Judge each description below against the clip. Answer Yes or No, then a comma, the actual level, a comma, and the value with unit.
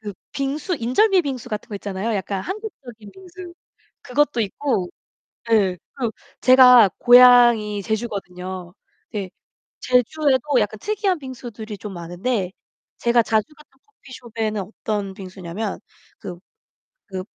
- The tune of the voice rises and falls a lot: No, average, 4.6 semitones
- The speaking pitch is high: Yes, high, 225 Hz